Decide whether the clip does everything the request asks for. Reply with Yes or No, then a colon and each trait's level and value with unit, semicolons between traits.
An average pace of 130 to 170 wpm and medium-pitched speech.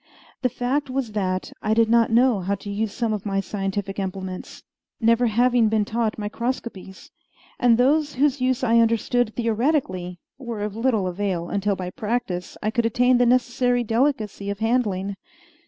No: average, 165 wpm; high, 225 Hz